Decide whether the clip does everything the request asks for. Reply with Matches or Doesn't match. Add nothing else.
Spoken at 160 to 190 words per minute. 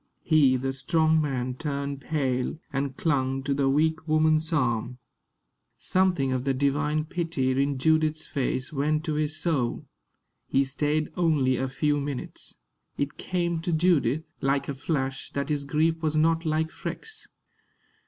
Doesn't match